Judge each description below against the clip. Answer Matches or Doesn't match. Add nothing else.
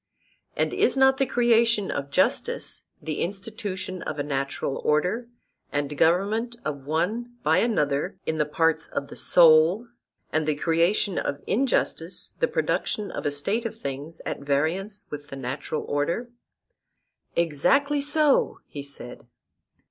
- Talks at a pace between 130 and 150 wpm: Matches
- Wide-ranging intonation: Matches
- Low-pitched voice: Doesn't match